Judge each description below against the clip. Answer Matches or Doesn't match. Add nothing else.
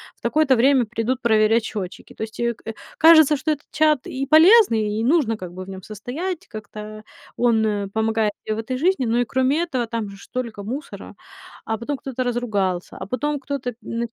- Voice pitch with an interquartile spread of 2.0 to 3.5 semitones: Doesn't match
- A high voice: Matches